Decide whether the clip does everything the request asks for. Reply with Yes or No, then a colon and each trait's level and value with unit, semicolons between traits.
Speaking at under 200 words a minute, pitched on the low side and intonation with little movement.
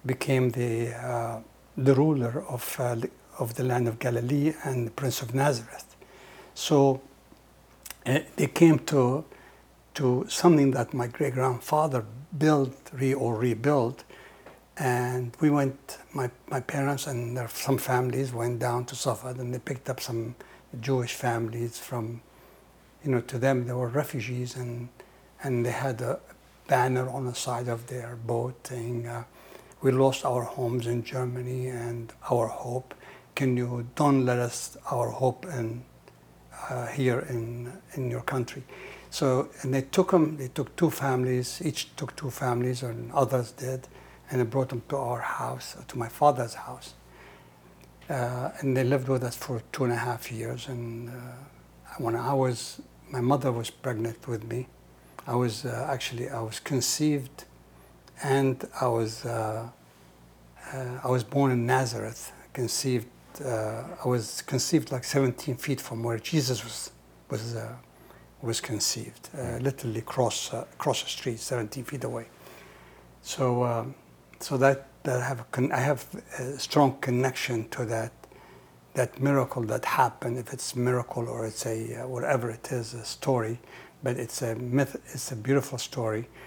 Yes: average, 160 wpm; low, 125 Hz; narrow, 2.3 semitones